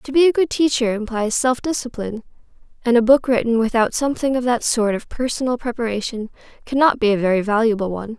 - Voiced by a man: No, female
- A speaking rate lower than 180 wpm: No, average, 190 wpm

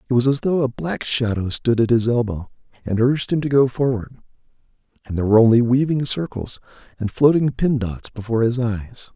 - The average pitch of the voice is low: Yes, low, 125 Hz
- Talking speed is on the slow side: No, average, 195 wpm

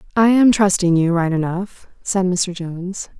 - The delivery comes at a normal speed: Yes, average, 170 wpm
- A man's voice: No, female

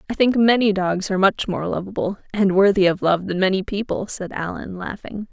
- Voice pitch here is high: Yes, high, 195 Hz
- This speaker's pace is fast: No, average, 180 wpm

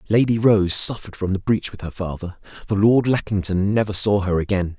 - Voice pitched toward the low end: Yes, low, 100 Hz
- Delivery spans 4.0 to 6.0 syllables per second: Yes, 5.5 syllables/s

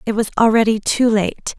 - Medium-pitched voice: No, high, 220 Hz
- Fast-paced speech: No, average, 190 wpm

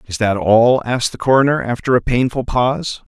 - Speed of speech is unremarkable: Yes, average, 190 wpm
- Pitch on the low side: Yes, low, 120 Hz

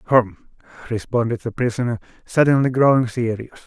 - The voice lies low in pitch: Yes, low, 120 Hz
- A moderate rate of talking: No, slow, 115 wpm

